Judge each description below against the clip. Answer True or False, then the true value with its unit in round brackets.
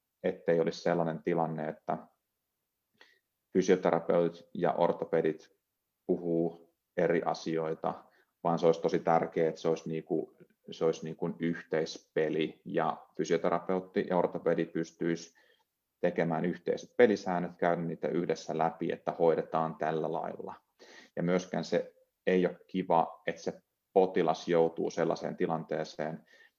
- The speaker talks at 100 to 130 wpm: True (120 wpm)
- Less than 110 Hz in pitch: True (85 Hz)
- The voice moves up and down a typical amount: False (1.1 semitones)